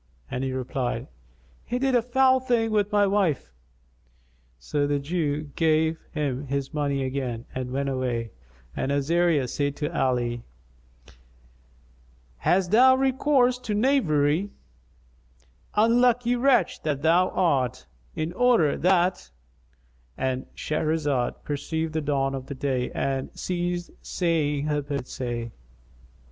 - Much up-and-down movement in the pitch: Yes, wide, 6.5 semitones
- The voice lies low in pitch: No, medium, 150 Hz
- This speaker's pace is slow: Yes, slow, 120 wpm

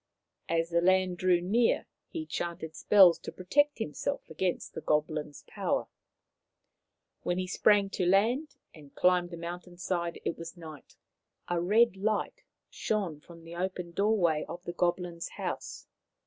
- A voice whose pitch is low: No, medium, 180 Hz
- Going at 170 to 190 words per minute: No, average, 150 wpm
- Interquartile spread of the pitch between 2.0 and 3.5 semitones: Yes, narrow, 2.6 semitones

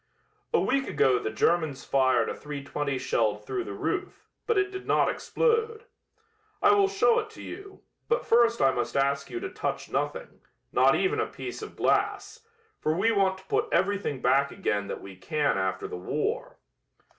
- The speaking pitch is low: No, medium, 175 Hz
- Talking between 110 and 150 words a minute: No, average, 180 wpm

